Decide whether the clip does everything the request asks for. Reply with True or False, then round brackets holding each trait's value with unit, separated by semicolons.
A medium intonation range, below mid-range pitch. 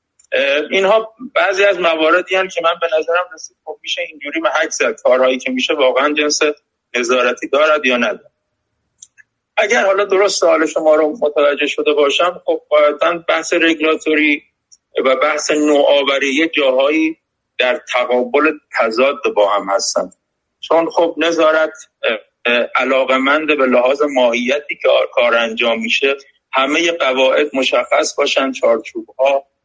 False (4.0 semitones; 150 Hz)